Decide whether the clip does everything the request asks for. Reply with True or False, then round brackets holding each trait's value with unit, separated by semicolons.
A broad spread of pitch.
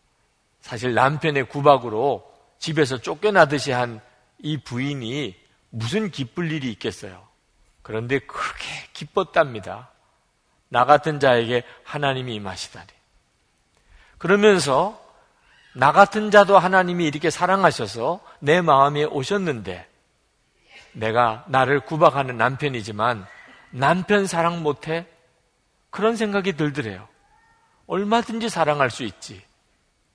True (6.0 semitones)